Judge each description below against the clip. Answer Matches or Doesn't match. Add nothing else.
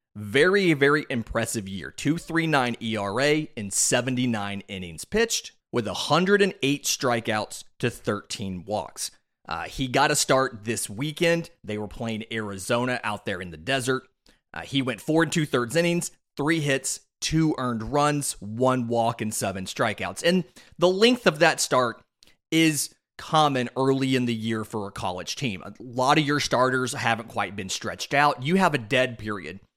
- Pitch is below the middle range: Matches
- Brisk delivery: Doesn't match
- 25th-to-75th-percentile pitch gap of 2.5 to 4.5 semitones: Doesn't match